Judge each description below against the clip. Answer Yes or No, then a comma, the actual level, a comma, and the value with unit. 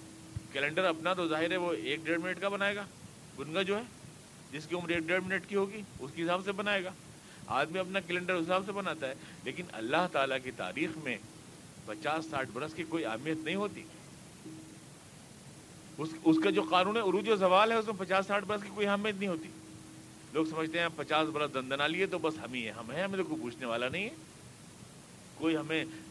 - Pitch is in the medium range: Yes, medium, 170 Hz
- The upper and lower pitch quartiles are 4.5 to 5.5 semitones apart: No, average, 3.8 semitones